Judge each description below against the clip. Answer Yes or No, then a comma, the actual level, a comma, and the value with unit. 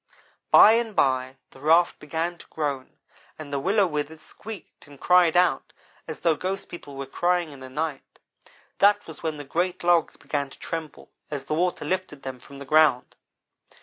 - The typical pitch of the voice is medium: Yes, medium, 160 Hz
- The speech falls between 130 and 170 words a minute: No, average, 180 wpm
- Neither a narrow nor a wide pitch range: Yes, average, 3.9 semitones